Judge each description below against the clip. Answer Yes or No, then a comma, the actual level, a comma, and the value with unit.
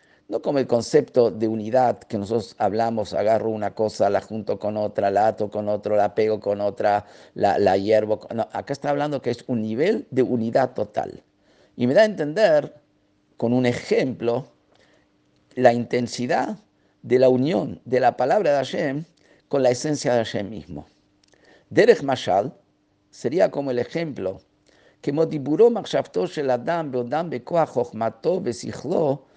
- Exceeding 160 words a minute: No, average, 145 wpm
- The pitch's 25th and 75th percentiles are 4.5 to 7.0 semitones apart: Yes, average, 4.9 semitones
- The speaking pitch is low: Yes, low, 120 Hz